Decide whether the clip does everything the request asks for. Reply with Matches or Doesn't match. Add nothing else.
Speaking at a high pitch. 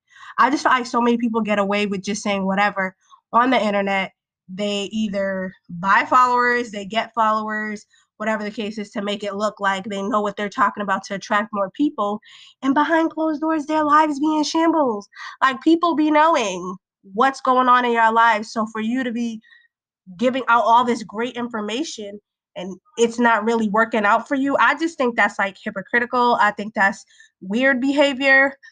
Matches